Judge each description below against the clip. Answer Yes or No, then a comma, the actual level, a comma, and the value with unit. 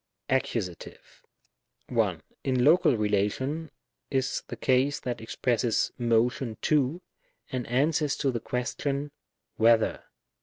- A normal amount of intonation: Yes, average, 3.4 semitones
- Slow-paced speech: Yes, slow, 110 wpm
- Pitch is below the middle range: Yes, low, 130 Hz